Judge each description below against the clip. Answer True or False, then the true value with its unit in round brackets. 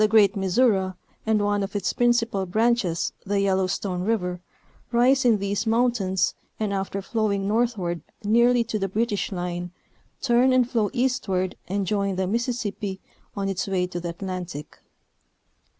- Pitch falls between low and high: False (200 Hz)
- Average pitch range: True (3.6 semitones)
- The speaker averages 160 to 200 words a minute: False (145 wpm)